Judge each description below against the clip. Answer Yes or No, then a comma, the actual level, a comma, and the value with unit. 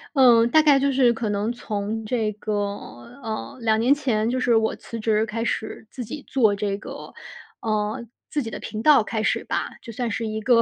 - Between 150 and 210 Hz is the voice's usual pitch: No, high, 225 Hz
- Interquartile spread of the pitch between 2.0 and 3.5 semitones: Yes, narrow, 2.6 semitones